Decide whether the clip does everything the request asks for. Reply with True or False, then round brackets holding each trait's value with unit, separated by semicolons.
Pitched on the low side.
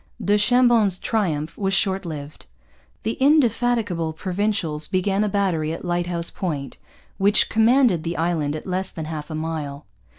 False (185 Hz)